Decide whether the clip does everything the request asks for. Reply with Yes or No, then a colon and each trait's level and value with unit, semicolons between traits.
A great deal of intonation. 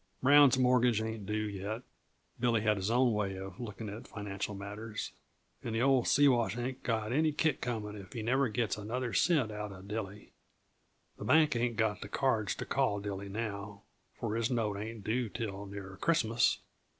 No: average, 3.1 semitones